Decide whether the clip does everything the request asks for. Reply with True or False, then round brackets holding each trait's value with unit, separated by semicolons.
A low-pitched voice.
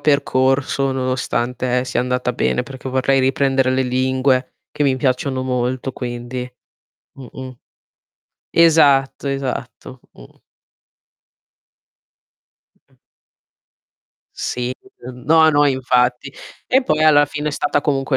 True (130 Hz)